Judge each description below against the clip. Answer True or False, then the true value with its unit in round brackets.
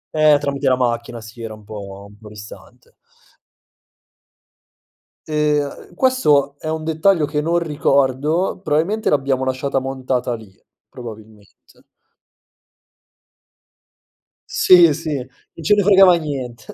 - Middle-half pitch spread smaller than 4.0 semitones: False (4.8 semitones)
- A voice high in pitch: False (140 Hz)